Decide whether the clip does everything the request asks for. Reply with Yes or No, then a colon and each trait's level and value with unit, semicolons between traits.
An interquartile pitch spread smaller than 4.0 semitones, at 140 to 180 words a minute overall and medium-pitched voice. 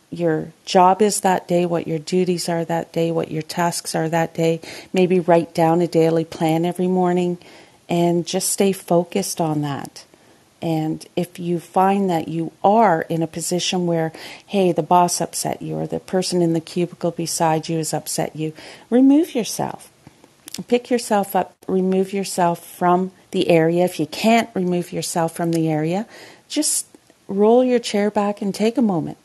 Yes: narrow, 2.4 semitones; average, 175 wpm; medium, 175 Hz